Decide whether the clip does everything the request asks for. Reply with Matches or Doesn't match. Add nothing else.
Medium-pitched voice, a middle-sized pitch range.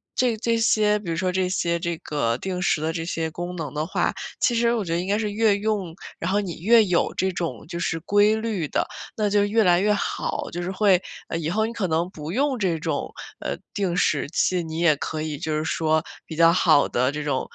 Matches